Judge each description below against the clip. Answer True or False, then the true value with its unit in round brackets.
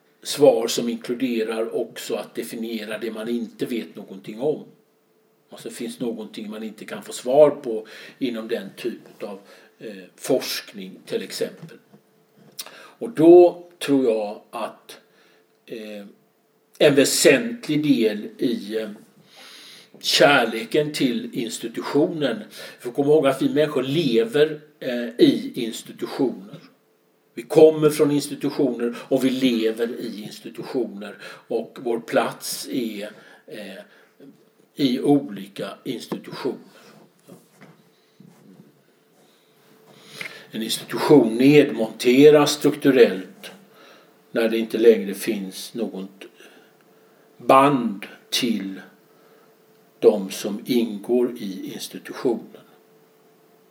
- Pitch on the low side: True (125 Hz)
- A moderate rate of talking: False (95 wpm)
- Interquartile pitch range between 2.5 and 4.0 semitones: False (5.1 semitones)